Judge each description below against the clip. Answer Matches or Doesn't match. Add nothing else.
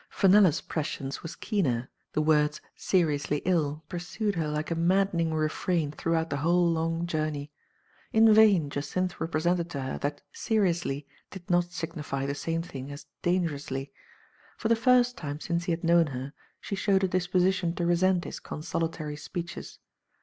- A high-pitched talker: Doesn't match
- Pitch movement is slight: Doesn't match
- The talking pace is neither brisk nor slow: Matches